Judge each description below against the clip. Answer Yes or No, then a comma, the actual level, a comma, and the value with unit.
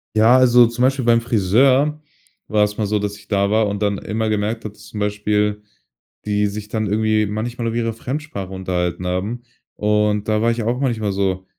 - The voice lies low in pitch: Yes, low, 105 Hz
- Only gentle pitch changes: Yes, narrow, 2.2 semitones